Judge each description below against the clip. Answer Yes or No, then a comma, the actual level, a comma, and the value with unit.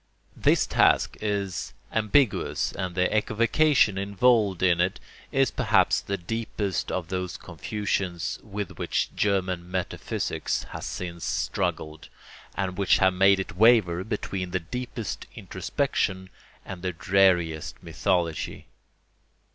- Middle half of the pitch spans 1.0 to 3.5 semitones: Yes, narrow, 2.6 semitones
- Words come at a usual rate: No, slow, 115 wpm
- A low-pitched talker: Yes, very low, 95 Hz